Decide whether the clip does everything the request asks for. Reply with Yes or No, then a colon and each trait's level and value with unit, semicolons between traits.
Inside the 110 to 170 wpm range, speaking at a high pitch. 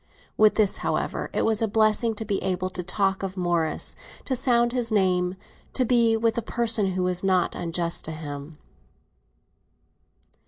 Yes: average, 165 wpm; high, 195 Hz